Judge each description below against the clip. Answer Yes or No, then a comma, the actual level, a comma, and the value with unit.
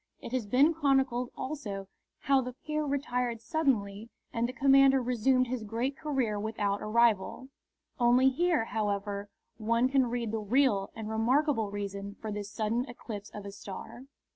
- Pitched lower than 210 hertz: No, high, 235 Hz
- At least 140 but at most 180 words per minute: Yes, average, 160 wpm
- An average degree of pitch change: Yes, average, 4.1 semitones